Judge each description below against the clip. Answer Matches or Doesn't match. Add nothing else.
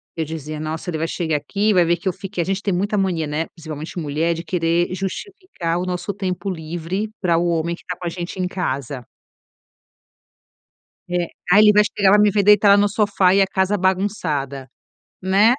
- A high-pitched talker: Doesn't match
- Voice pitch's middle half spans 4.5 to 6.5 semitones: Doesn't match